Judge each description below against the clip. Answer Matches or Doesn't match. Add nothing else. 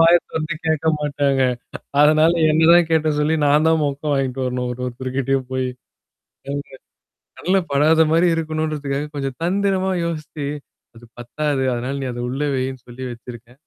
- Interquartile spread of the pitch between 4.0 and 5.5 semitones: Doesn't match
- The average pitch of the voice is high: Doesn't match